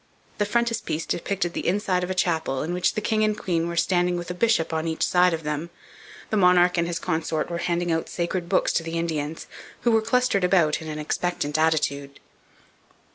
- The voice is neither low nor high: Yes, medium, 175 Hz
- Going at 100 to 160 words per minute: No, average, 200 wpm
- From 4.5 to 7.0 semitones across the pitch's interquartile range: No, narrow, 2.4 semitones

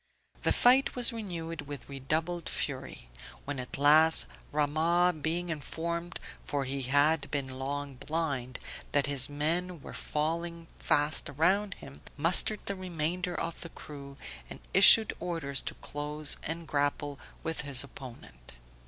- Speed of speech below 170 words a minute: Yes, slow, 135 wpm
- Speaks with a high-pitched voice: No, medium, 155 Hz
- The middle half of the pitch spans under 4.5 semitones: Yes, average, 3.1 semitones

